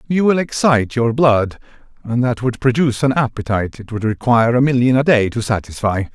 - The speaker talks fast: No, average, 195 wpm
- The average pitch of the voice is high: No, low, 120 Hz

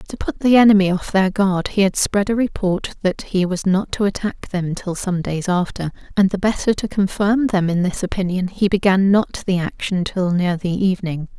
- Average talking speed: No, fast, 215 wpm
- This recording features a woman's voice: Yes, female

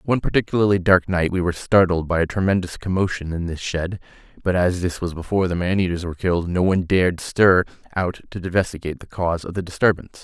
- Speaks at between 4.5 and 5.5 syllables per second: No, 6.6 syllables/s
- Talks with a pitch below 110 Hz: Yes, very low, 90 Hz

